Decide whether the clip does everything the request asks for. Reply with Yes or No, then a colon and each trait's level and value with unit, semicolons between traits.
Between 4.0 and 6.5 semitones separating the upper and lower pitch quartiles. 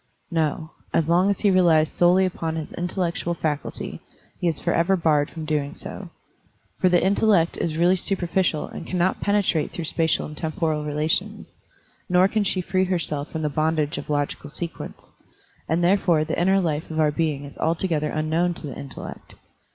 No: average, 2.7 semitones